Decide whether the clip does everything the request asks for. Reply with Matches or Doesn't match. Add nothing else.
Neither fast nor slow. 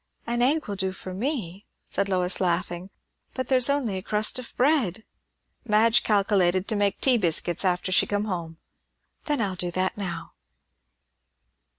Matches